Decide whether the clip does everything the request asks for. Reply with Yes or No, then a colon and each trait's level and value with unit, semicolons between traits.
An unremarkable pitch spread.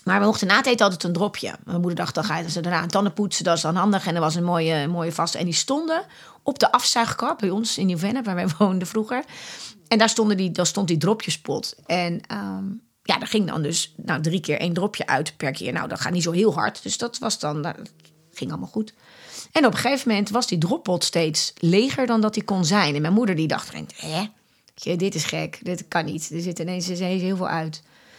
Yes: average, 3.9 semitones